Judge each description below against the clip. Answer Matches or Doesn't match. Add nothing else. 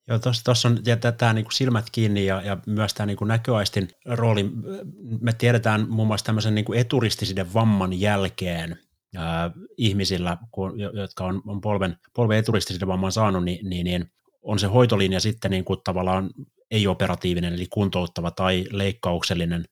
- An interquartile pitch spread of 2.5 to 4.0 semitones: Matches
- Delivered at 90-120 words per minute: Doesn't match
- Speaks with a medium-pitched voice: Doesn't match